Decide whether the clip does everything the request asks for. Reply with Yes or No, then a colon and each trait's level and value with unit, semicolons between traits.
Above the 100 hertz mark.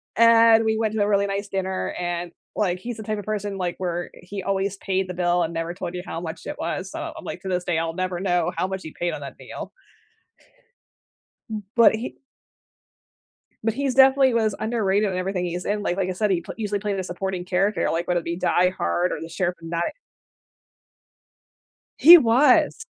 Yes: high, 190 Hz